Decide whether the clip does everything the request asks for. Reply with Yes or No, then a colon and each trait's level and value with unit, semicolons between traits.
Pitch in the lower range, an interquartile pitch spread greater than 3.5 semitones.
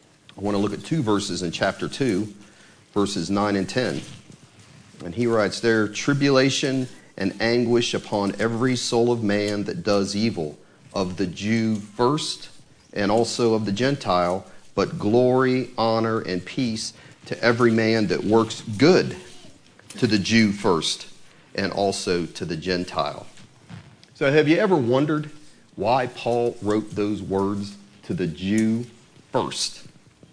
No: low, 110 Hz; average, 3.1 semitones